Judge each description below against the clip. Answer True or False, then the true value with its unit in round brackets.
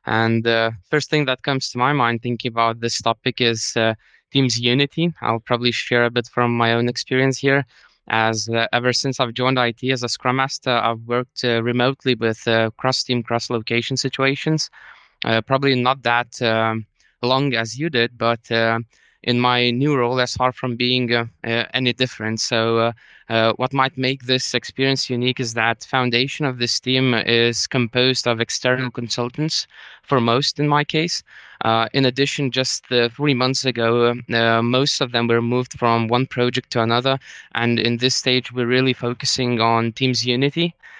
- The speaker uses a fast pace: False (185 wpm)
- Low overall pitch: True (125 Hz)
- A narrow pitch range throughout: True (1.9 semitones)